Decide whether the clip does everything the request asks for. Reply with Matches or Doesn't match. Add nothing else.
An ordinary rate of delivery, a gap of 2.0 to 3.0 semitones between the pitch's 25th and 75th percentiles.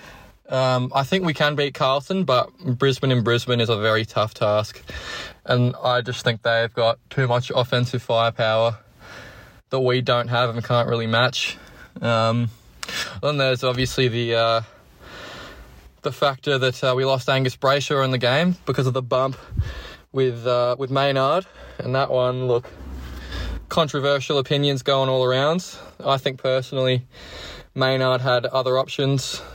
Matches